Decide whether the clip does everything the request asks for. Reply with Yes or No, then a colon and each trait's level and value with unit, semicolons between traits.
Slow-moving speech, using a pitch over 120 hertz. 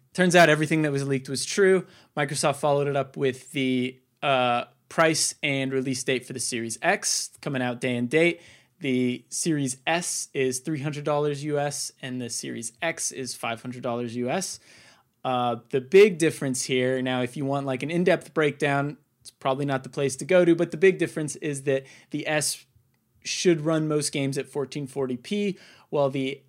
No: average, 175 wpm; medium, 140 Hz